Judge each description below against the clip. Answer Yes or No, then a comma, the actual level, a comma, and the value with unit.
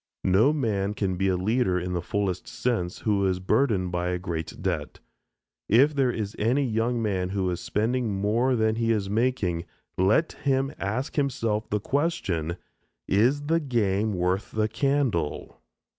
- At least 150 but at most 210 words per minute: Yes, average, 160 wpm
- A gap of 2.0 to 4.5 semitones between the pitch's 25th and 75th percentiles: No, average, 5.1 semitones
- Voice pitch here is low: Yes, low, 105 Hz